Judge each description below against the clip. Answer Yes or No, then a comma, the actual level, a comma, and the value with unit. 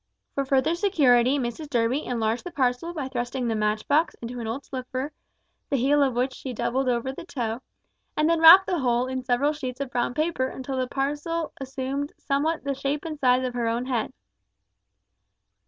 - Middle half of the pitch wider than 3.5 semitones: No, average, 3.0 semitones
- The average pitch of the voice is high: Yes, very high, 265 Hz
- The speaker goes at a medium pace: Yes, average, 190 wpm